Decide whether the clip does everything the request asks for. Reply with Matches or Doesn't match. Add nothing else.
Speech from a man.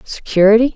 Doesn't match